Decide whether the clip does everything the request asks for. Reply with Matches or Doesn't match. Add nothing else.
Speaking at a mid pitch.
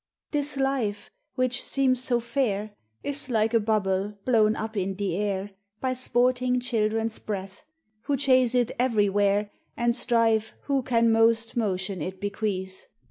Doesn't match